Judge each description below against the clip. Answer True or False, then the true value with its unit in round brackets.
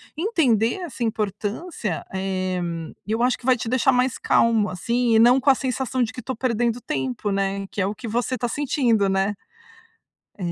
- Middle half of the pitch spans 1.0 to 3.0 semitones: False (3.9 semitones)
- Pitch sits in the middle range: False (230 Hz)